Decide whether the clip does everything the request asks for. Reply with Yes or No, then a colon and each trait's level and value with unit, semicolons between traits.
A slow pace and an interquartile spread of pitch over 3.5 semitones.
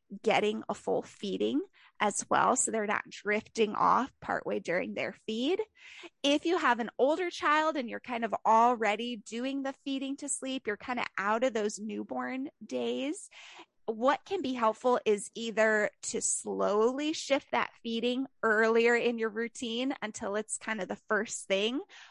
No: average, 165 wpm; average, 4.1 semitones